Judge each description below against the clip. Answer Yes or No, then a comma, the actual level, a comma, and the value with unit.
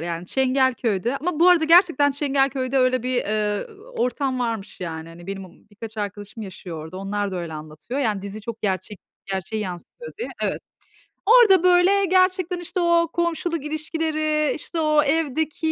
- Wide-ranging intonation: Yes, wide, 8.1 semitones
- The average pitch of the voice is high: Yes, very high, 260 Hz